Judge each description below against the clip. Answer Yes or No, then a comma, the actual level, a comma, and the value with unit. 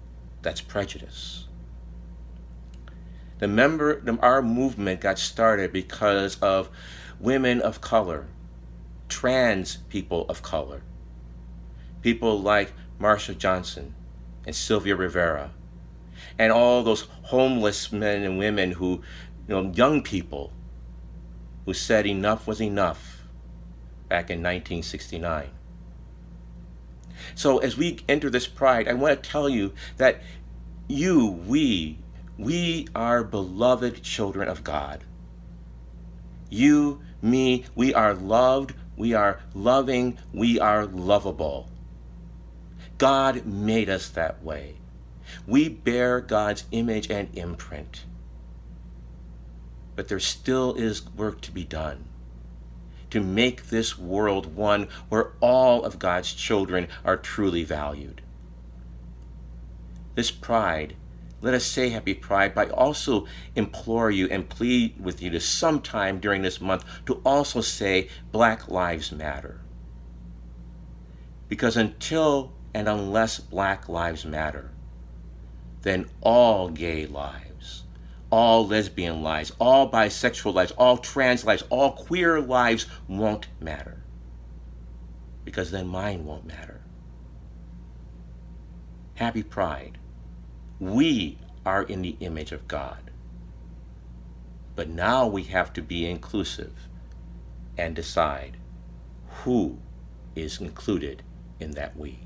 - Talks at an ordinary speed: No, slow, 110 wpm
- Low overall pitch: Yes, very low, 80 Hz